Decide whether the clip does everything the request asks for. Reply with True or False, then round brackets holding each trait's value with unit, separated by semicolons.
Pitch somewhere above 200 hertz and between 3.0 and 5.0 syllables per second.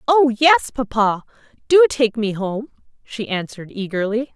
True (235 Hz; 4.5 syllables/s)